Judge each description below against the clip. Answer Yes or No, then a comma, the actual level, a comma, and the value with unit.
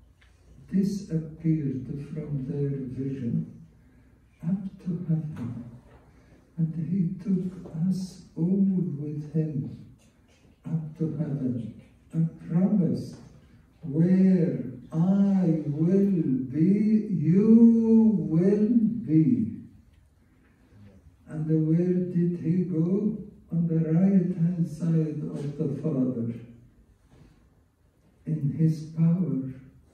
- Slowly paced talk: Yes, slow, 85 wpm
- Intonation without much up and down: No, average, 5.2 semitones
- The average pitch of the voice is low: No, medium, 160 Hz